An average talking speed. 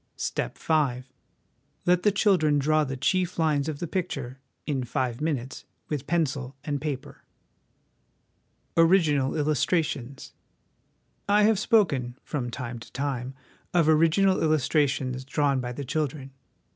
No: slow, 130 wpm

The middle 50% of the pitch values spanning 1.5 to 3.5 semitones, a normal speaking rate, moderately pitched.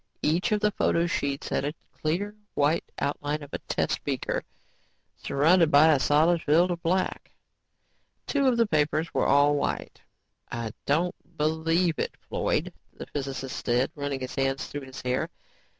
Yes: average, 3.2 semitones; average, 160 wpm; medium, 150 Hz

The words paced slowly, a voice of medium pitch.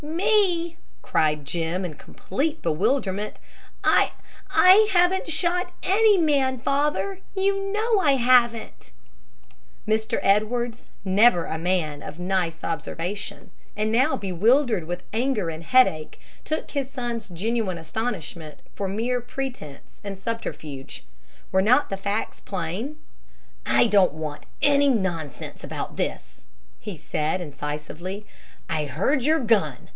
No: slow, 120 wpm; high, 215 Hz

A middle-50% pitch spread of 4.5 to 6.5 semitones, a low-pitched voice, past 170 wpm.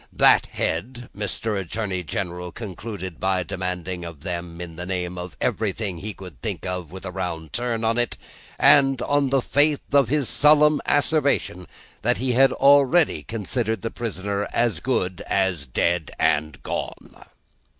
No: wide, 5.5 semitones; low, 100 Hz; average, 150 wpm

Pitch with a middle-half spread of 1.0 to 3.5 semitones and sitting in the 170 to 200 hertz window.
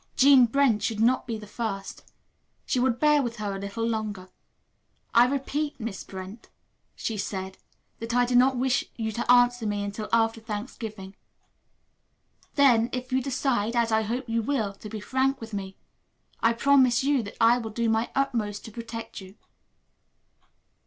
No: average, 3.0 semitones; high, 230 Hz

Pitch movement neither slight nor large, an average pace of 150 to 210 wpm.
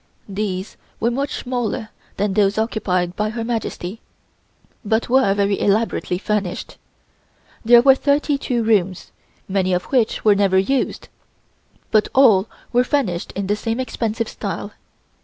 No: average, 3.5 semitones; average, 140 wpm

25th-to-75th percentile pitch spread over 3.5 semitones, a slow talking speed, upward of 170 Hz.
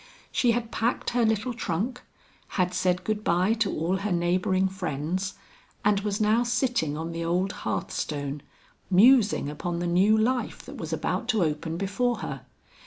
No: average, 4.4 semitones; average, 165 wpm; high, 190 Hz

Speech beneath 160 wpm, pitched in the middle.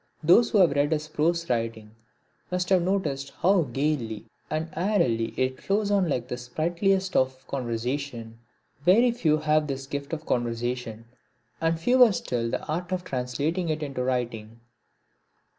Yes: average, 150 wpm; medium, 150 Hz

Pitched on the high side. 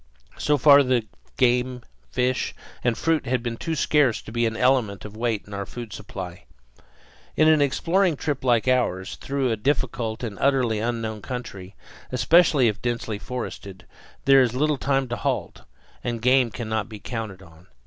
No: low, 120 Hz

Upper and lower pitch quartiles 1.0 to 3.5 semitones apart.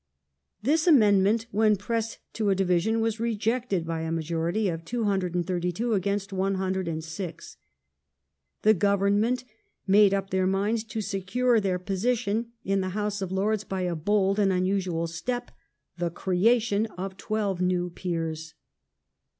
Yes: average, 3.2 semitones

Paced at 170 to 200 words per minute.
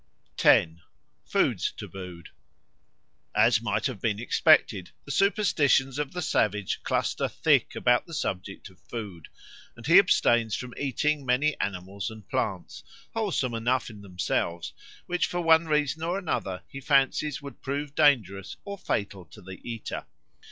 No: average, 145 wpm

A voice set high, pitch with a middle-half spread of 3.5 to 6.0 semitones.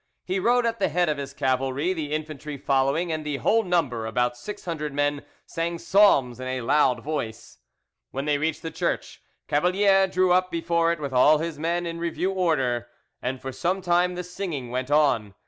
No: medium, 155 Hz; average, 4.9 semitones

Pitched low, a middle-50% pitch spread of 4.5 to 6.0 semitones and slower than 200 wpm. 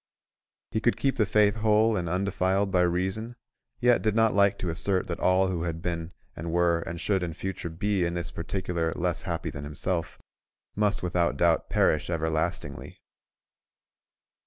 No: very low, 90 Hz; average, 3.1 semitones; average, 165 wpm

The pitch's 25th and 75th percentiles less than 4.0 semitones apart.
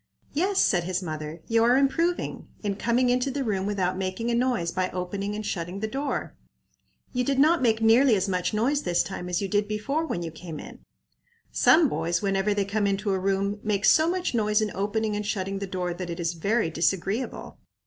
No: average, 4.4 semitones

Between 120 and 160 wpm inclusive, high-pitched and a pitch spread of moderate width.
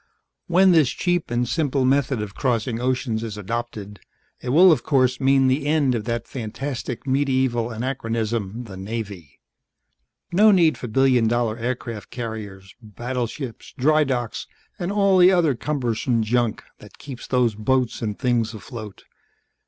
No: average, 145 wpm; low, 125 Hz; average, 3.4 semitones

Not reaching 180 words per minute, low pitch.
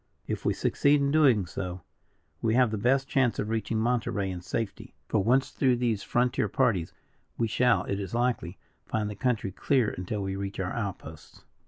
No: average, 185 wpm; low, 110 Hz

